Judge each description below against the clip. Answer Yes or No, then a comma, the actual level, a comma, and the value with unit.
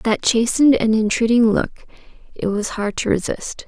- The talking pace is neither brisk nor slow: Yes, average, 165 wpm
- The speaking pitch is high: Yes, high, 225 Hz